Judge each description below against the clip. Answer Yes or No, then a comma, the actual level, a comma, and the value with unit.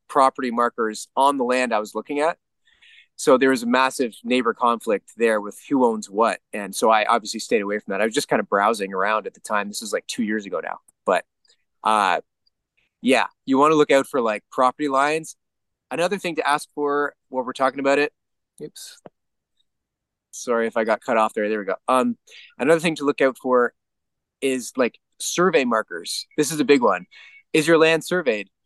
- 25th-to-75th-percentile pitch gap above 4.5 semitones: Yes, average, 4.9 semitones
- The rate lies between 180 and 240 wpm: Yes, fast, 205 wpm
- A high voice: No, low, 130 Hz